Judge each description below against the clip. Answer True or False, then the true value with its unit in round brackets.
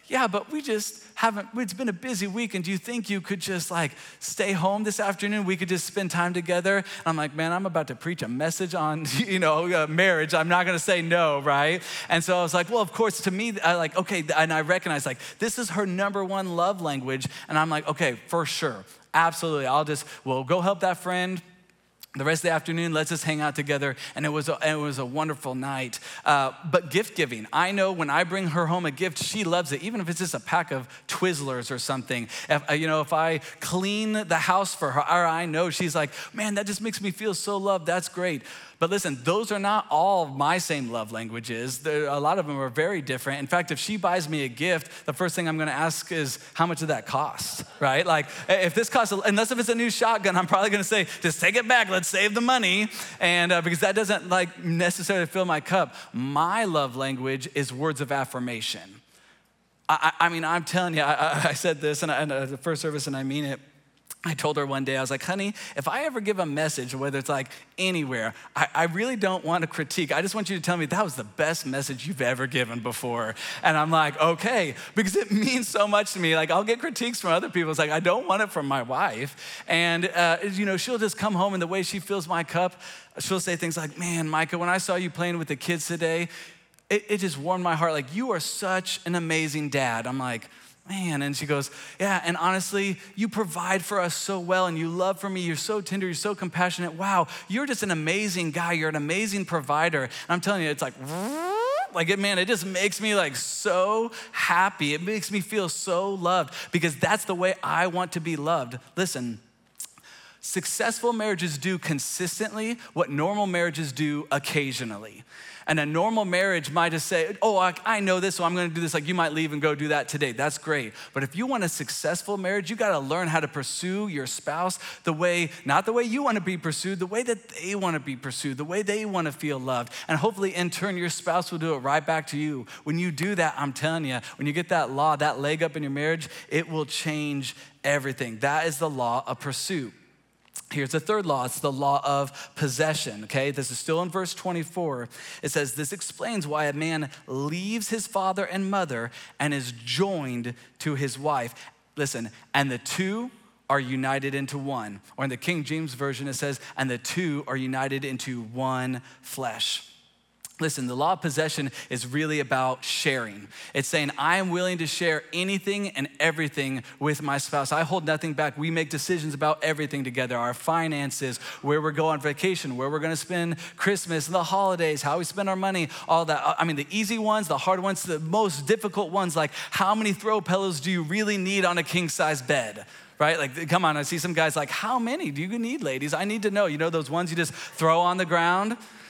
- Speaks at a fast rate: True (225 wpm)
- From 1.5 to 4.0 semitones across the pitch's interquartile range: False (4.5 semitones)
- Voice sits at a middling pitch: True (170 Hz)